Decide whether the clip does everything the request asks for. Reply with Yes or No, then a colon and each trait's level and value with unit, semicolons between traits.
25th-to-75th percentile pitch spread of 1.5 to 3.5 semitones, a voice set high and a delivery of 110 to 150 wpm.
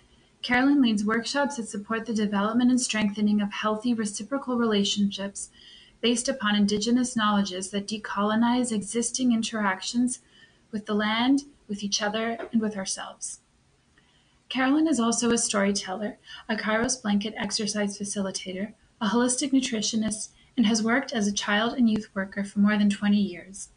Yes: narrow, 2.4 semitones; high, 215 Hz; average, 145 wpm